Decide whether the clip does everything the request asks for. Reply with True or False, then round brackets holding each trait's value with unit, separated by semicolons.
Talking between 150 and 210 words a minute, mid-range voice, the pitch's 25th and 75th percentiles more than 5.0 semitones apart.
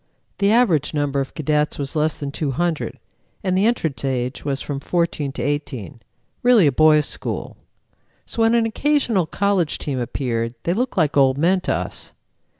True (170 wpm; 150 Hz; 5.5 semitones)